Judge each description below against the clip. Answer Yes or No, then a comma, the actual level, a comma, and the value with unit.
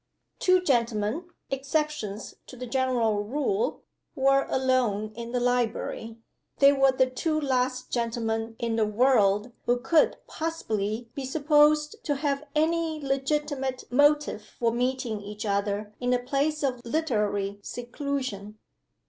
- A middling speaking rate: No, slow, 130 wpm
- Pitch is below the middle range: No, very high, 255 Hz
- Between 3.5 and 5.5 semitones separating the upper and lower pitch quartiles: Yes, average, 4.2 semitones